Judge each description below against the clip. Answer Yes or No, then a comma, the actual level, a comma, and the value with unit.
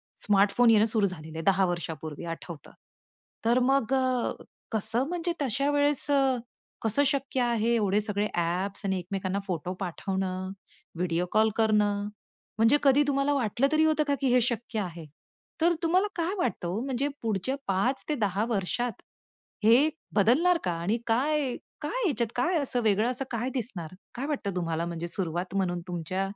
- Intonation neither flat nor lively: No, wide, 6.2 semitones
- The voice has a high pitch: Yes, high, 220 Hz